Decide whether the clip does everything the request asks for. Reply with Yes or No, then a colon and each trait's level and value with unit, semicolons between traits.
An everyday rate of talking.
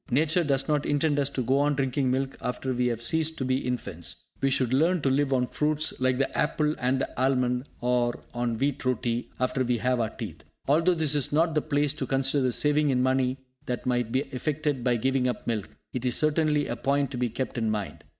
No: fast, 230 wpm